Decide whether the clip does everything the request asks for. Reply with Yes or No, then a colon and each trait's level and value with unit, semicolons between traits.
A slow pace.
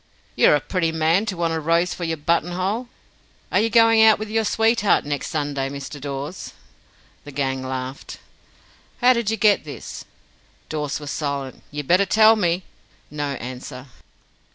No: average, 160 wpm